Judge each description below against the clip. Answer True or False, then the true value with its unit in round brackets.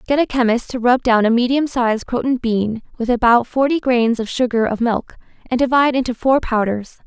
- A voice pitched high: True (240 Hz)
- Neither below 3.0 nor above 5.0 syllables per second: False (5.4 syllables/s)